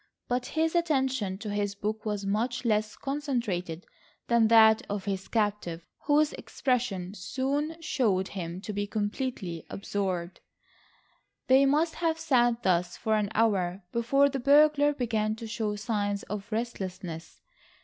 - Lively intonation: No, average, 4.7 semitones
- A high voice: Yes, high, 220 Hz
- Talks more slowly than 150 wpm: Yes, average, 140 wpm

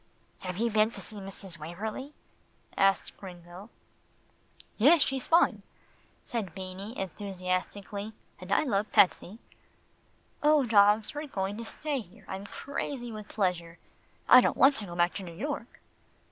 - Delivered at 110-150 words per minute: Yes, average, 145 wpm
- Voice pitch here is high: Yes, high, 205 Hz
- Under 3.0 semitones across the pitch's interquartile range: No, average, 4.2 semitones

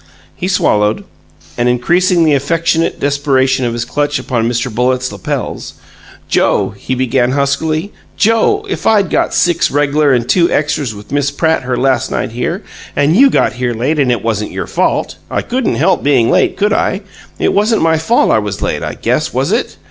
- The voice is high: No, medium, 140 Hz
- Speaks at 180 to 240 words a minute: Yes, average, 185 wpm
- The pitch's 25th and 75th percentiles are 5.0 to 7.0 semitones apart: Yes, wide, 5.4 semitones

